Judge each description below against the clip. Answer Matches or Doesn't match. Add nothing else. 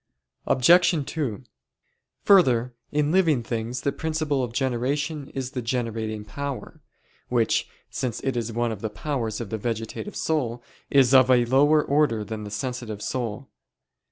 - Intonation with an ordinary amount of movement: Matches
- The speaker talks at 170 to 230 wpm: Doesn't match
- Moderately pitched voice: Doesn't match